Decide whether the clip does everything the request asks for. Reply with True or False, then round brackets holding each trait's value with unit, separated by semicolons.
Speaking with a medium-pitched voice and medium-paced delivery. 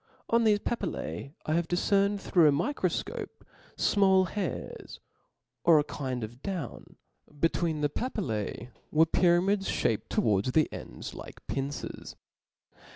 False (165 Hz; 130 wpm)